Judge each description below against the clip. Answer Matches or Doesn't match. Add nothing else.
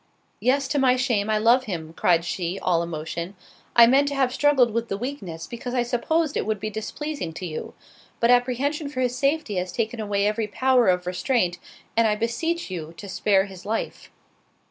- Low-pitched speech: Doesn't match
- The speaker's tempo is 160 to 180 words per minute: Doesn't match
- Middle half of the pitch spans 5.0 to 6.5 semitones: Matches